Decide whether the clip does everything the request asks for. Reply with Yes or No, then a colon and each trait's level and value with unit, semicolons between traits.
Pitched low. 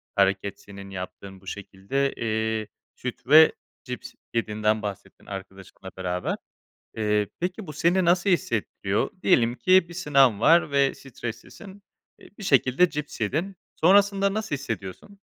Yes: low, 125 Hz